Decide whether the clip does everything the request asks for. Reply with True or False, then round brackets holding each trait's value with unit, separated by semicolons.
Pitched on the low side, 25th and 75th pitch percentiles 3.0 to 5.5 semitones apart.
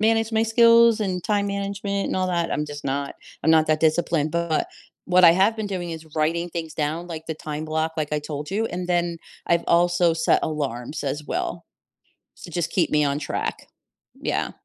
False (170 Hz; 3.4 semitones)